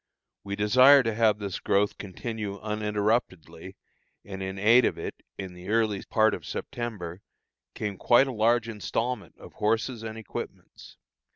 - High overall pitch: No, low, 105 Hz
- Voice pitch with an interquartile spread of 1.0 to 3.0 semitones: Yes, narrow, 2.4 semitones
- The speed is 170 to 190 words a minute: No, average, 150 wpm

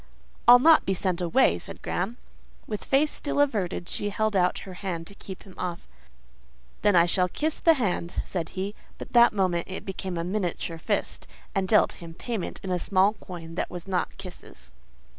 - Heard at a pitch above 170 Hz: Yes, high, 190 Hz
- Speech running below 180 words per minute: No, average, 190 wpm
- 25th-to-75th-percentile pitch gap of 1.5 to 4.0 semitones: Yes, average, 3.3 semitones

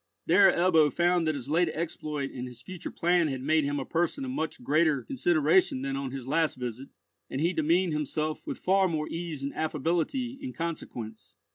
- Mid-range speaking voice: Yes, medium, 155 Hz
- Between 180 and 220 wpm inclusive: Yes, average, 190 wpm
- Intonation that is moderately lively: Yes, average, 3.8 semitones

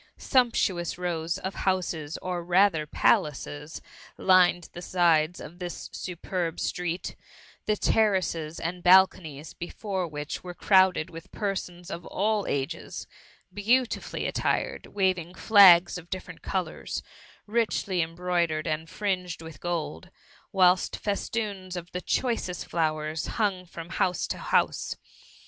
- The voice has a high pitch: No, medium, 180 Hz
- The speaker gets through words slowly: Yes, slow, 130 wpm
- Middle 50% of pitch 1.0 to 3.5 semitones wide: Yes, narrow, 2.4 semitones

